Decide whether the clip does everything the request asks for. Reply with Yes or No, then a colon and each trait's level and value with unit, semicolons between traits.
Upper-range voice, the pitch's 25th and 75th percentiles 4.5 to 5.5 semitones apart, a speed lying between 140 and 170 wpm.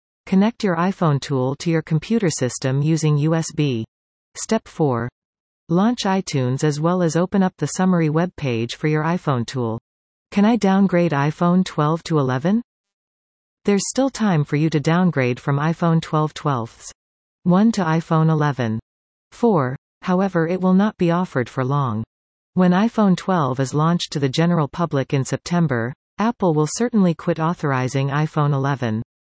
No: medium, 160 Hz; average, 5.1 semitones; average, 155 wpm